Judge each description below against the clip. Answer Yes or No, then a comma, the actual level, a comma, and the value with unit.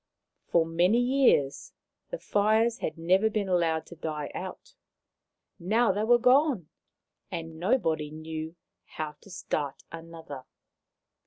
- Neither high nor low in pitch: Yes, medium, 175 Hz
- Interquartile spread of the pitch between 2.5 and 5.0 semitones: No, wide, 5.6 semitones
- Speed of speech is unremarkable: No, slow, 120 wpm